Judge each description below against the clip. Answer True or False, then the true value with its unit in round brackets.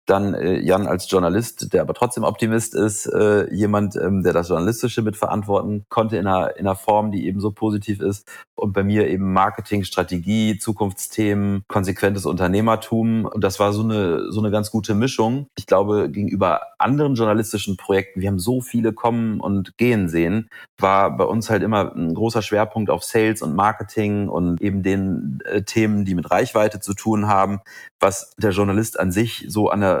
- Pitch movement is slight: True (2.1 semitones)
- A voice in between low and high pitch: False (105 Hz)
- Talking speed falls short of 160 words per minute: False (170 wpm)